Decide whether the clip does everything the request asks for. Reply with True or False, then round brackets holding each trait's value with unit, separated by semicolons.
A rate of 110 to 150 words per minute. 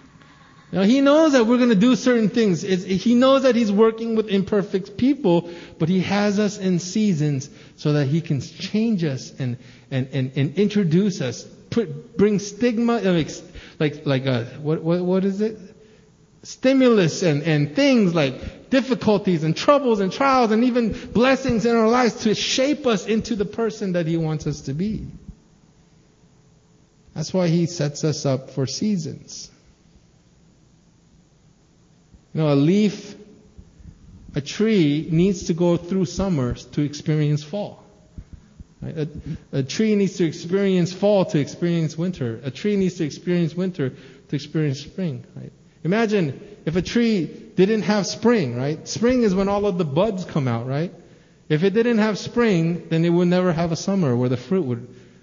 False (160 wpm)